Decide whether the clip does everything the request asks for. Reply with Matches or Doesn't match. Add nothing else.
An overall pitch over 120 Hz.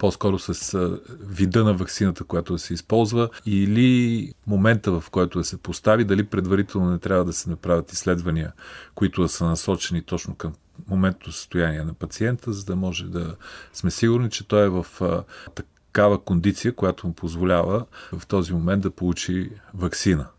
Doesn't match